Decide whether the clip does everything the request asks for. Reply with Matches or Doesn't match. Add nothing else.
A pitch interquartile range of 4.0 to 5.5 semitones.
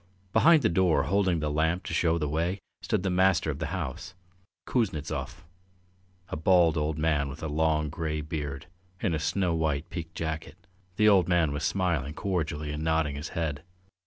Doesn't match